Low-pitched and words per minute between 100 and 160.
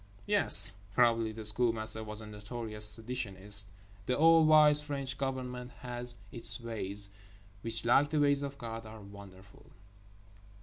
Yes: low, 115 Hz; slow, 135 wpm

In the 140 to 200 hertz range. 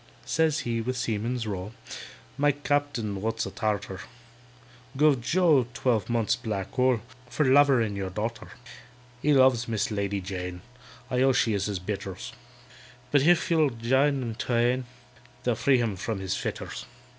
No: low, 120 Hz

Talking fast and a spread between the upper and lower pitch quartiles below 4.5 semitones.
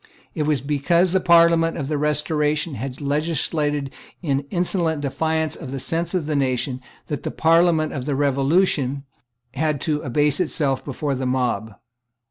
No: average, 155 wpm; average, 3.0 semitones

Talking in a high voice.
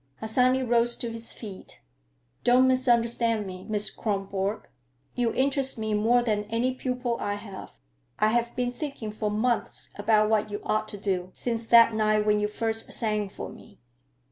Yes: high, 225 Hz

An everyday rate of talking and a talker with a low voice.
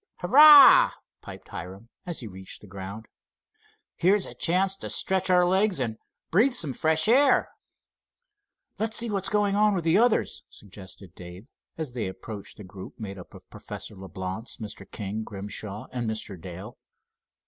Yes: average, 160 wpm; low, 115 Hz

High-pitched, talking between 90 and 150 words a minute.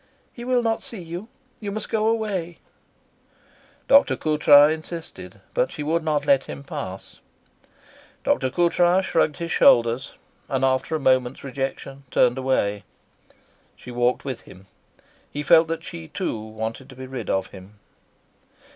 No: medium, 145 Hz; average, 145 wpm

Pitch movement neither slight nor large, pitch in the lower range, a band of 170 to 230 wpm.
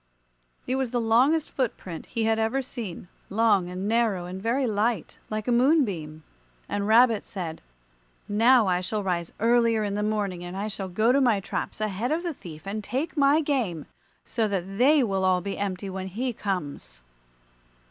No: average, 4.3 semitones; high, 215 Hz; average, 185 wpm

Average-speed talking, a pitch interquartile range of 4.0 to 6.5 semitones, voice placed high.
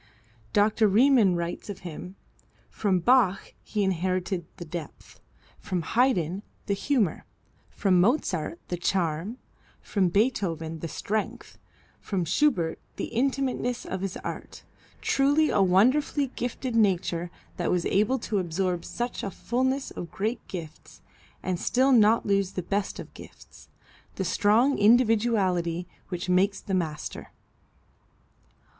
No: slow, 125 wpm; average, 4.9 semitones; high, 195 Hz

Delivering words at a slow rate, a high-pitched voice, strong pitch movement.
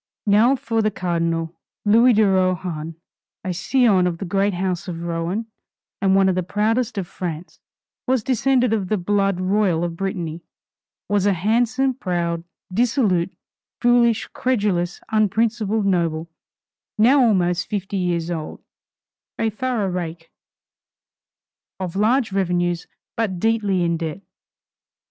No: slow, 125 wpm; high, 195 Hz; average, 4.1 semitones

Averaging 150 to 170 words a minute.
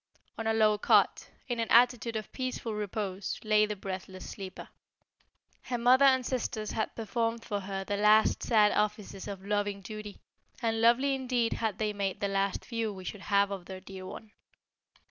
No: average, 180 wpm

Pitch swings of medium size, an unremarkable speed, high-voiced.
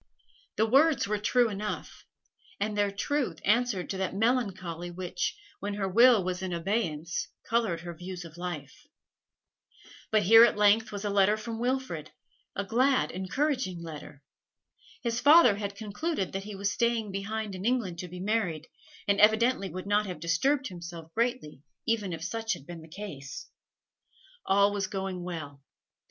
Yes: average, 4.2 semitones; average, 160 wpm; high, 200 Hz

